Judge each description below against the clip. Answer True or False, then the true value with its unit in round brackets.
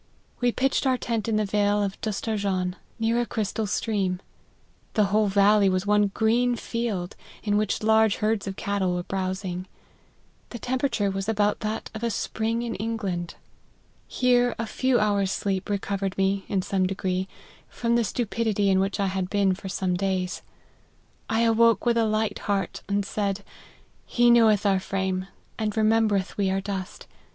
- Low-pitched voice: False (205 Hz)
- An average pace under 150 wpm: False (165 wpm)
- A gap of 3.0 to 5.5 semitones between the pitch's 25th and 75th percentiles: False (2.6 semitones)